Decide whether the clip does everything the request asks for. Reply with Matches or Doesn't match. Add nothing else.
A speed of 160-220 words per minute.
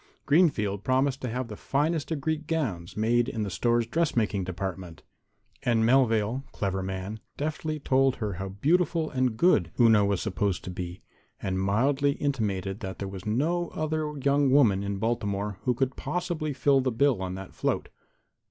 Matches